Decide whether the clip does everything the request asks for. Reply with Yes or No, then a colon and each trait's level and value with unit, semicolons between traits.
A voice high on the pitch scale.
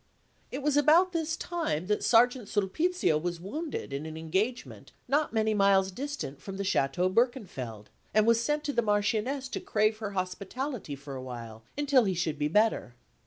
Yes: high, 210 Hz